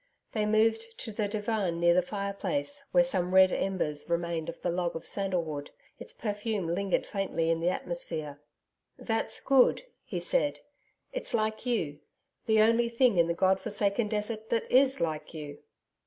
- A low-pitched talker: No, high, 200 Hz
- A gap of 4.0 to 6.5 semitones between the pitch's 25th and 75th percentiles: Yes, average, 4.7 semitones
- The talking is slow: No, average, 165 wpm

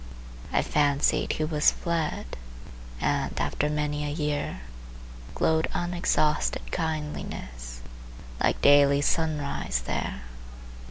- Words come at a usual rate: No, slow, 95 wpm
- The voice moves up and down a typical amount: No, narrow, 1.8 semitones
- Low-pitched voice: No, medium, 150 Hz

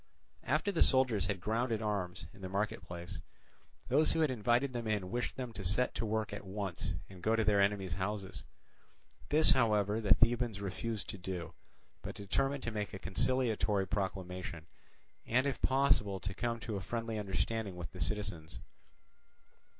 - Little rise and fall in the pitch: No, average, 3.6 semitones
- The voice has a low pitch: Yes, low, 105 Hz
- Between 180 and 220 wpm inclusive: No, average, 170 wpm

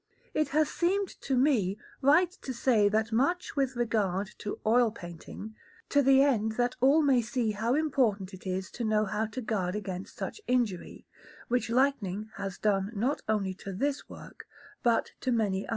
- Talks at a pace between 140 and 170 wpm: No, average, 180 wpm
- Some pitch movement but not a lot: Yes, average, 4.7 semitones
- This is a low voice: No, high, 225 Hz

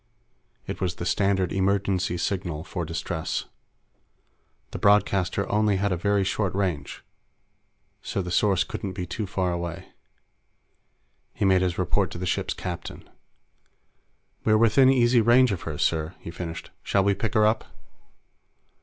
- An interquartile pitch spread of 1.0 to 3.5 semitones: Yes, average, 2.8 semitones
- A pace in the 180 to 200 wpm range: No, average, 145 wpm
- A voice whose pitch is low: Yes, very low, 95 Hz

